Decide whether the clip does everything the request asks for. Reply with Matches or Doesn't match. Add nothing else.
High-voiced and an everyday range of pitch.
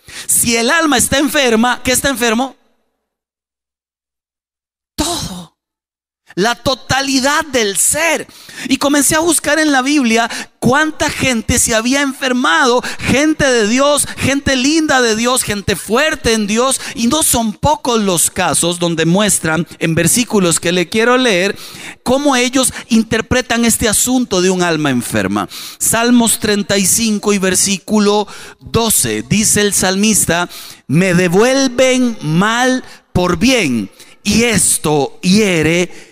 Doesn't match